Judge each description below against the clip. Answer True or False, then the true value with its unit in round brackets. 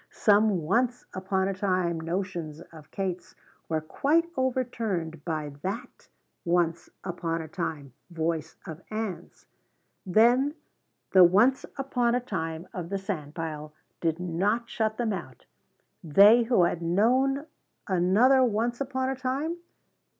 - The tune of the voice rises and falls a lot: True (6.2 semitones)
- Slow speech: True (130 wpm)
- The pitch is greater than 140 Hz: True (190 Hz)